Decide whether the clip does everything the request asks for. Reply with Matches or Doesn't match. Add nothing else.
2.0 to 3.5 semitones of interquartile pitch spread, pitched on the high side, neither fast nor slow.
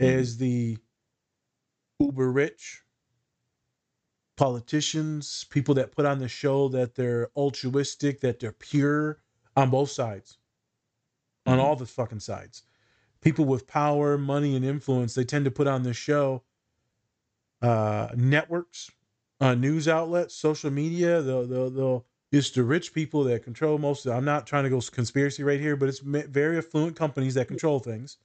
Doesn't match